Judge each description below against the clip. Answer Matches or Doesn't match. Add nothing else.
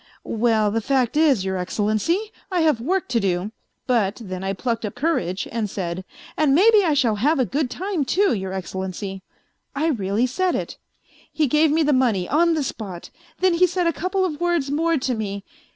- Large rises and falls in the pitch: Matches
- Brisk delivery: Matches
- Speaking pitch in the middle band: Doesn't match